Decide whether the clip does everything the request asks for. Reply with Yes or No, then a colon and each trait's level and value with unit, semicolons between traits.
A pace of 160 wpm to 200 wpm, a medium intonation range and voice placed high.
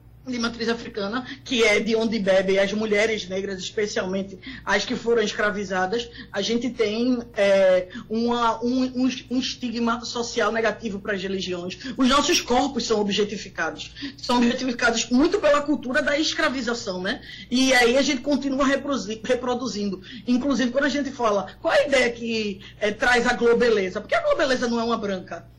Yes: average, 165 wpm; average, 3.6 semitones; high, 235 Hz